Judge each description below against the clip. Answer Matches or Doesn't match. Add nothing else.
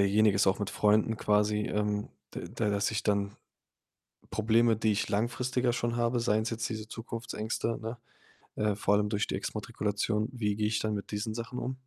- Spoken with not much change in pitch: Matches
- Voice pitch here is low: Matches